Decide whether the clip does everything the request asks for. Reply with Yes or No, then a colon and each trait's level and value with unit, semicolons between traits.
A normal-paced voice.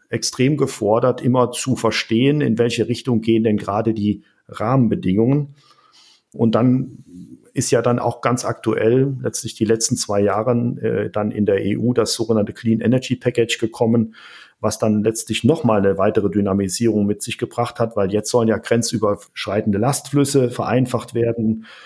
Yes: average, 155 wpm